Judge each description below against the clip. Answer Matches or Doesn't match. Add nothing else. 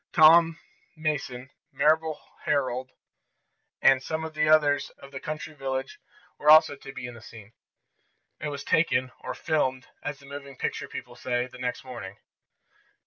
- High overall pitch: Doesn't match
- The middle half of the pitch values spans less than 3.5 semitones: Matches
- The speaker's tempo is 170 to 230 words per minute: Doesn't match